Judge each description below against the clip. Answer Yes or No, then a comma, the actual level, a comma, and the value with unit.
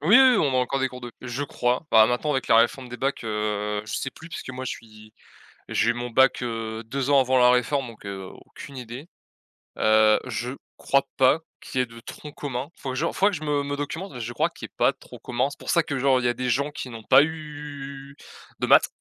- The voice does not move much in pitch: No, average, 3.3 semitones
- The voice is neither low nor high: No, low, 130 Hz